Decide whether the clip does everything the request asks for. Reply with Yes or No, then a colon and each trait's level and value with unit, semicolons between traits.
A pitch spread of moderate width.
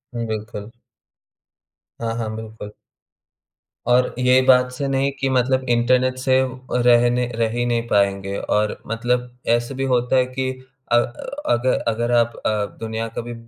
No: narrow, 2.0 semitones